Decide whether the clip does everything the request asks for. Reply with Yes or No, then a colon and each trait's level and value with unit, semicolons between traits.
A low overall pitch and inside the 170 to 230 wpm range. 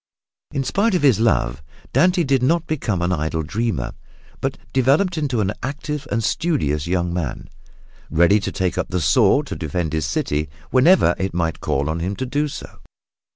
Yes: low, 100 Hz; average, 180 wpm